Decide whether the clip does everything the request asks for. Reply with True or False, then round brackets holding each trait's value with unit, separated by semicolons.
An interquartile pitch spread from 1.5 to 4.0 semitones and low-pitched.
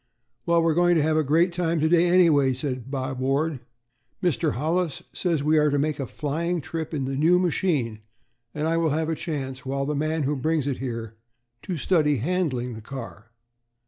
False (3.7 semitones; 150 Hz)